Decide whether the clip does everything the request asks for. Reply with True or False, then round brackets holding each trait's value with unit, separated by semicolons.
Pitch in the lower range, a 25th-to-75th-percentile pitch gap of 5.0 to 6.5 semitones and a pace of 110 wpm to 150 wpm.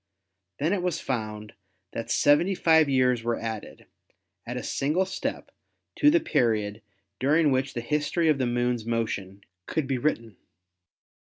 True (130 Hz; 5.3 semitones; 145 wpm)